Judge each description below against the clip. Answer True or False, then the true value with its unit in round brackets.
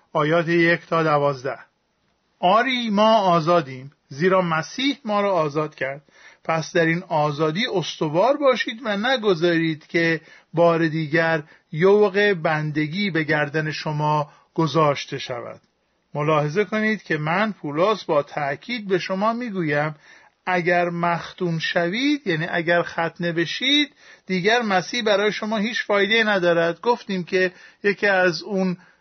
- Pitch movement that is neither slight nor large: True (4.4 semitones)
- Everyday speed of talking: True (125 wpm)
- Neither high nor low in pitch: True (175 Hz)